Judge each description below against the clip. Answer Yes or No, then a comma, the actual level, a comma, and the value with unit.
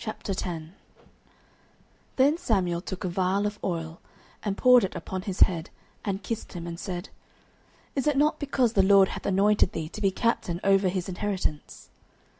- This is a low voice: No, high, 195 Hz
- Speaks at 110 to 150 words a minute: No, average, 165 wpm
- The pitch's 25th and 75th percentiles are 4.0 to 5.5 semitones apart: No, average, 3.1 semitones